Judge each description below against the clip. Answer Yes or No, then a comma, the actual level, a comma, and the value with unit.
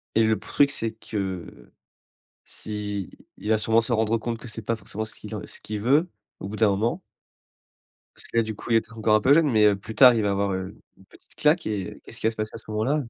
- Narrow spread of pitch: Yes, narrow, 1.8 semitones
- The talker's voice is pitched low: Yes, low, 110 Hz